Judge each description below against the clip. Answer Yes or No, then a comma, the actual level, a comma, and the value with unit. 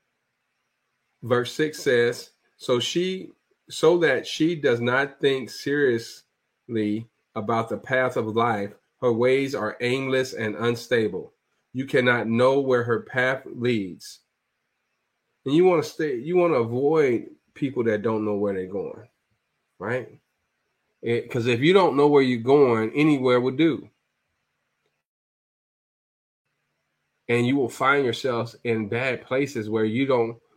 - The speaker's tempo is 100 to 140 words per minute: Yes, slow, 135 wpm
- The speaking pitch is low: Yes, low, 125 Hz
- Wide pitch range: No, average, 3.3 semitones